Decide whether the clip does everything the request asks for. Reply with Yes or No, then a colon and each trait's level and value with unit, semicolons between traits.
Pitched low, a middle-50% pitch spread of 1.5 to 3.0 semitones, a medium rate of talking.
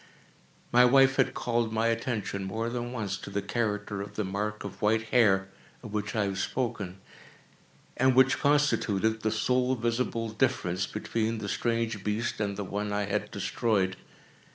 Yes: low, 110 Hz; average, 2.7 semitones; average, 165 wpm